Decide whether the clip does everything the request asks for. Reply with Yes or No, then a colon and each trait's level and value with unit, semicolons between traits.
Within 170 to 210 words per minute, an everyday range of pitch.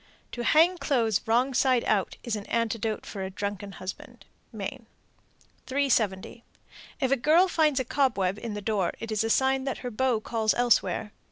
Yes: average, 175 wpm; average, 4.1 semitones